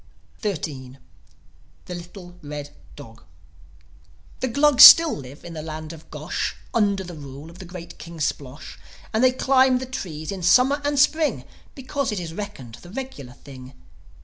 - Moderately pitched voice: Yes, medium, 175 Hz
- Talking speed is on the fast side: No, average, 165 wpm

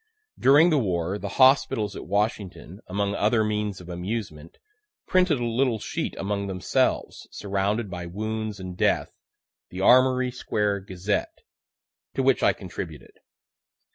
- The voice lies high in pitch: No, low, 105 Hz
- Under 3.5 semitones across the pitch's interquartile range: No, average, 3.9 semitones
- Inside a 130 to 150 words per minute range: Yes, slow, 135 wpm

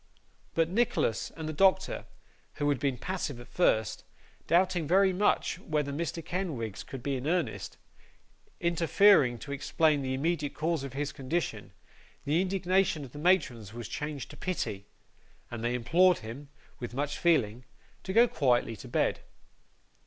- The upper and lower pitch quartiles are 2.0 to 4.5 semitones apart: No, average, 5.3 semitones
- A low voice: No, medium, 150 Hz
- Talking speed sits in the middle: Yes, average, 155 wpm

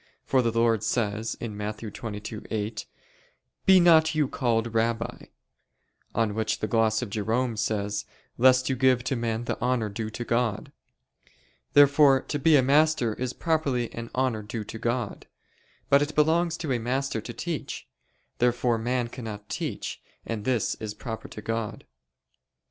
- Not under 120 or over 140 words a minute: No, average, 155 wpm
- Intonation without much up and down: No, average, 3.0 semitones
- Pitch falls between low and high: No, low, 115 Hz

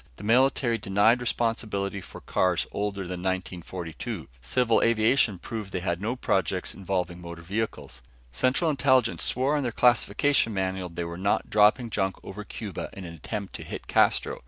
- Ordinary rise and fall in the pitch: Yes, average, 4.2 semitones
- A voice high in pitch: No, low, 100 Hz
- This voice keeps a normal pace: Yes, average, 160 wpm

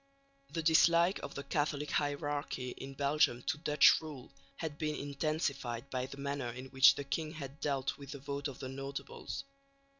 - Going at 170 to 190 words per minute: Yes, average, 175 wpm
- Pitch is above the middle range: No, medium, 140 Hz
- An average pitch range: No, narrow, 1.9 semitones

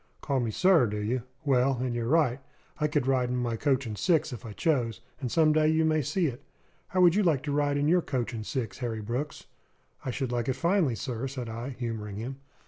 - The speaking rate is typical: No, fast, 235 wpm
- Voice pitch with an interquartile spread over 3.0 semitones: Yes, average, 4.2 semitones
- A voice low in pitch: Yes, low, 130 Hz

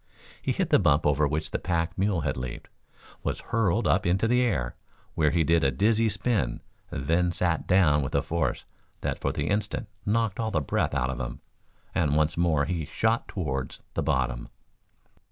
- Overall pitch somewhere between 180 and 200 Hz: No, very low, 85 Hz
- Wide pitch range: Yes, wide, 5.9 semitones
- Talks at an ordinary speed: Yes, average, 190 wpm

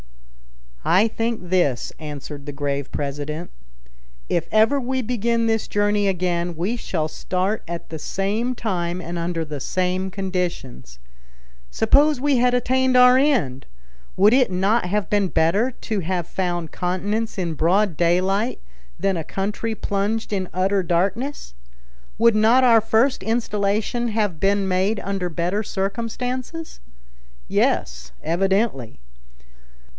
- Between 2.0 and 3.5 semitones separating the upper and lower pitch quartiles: No, average, 4.6 semitones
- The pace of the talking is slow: Yes, slow, 130 wpm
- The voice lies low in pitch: No, high, 195 Hz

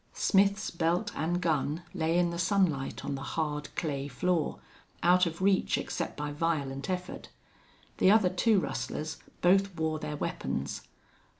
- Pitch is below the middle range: No, medium, 170 Hz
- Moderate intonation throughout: Yes, average, 3.6 semitones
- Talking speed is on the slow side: No, average, 145 wpm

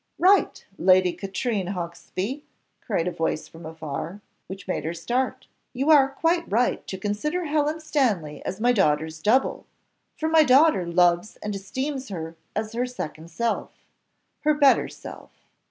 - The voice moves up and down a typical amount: No, wide, 7.9 semitones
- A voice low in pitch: No, high, 210 Hz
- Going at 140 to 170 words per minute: Yes, average, 150 wpm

